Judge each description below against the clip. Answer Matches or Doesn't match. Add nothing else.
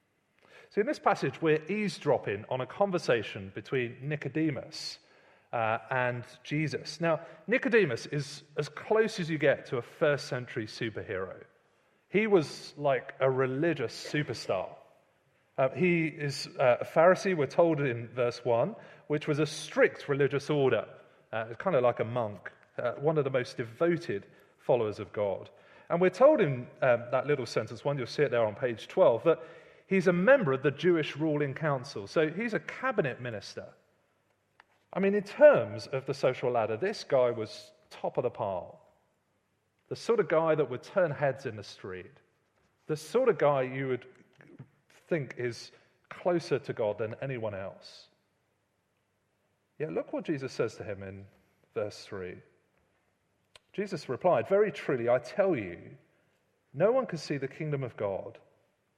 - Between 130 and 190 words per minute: Matches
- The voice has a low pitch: Doesn't match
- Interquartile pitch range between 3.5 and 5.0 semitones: Doesn't match